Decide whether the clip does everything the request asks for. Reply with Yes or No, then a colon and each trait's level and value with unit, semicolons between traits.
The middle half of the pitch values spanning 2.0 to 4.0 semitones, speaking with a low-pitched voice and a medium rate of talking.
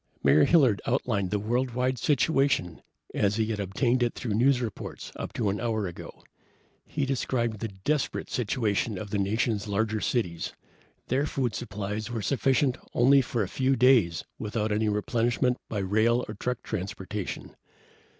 Yes: average, 3.5 semitones; low, 115 Hz; average, 155 wpm